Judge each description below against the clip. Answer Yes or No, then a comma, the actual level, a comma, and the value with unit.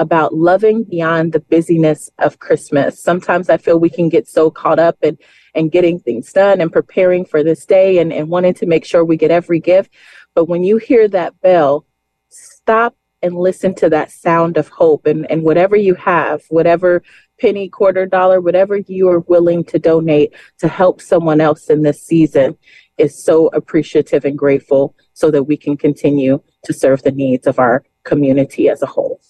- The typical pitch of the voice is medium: Yes, medium, 170 Hz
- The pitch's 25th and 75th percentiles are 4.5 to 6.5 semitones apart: No, average, 3.3 semitones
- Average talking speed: Yes, average, 190 wpm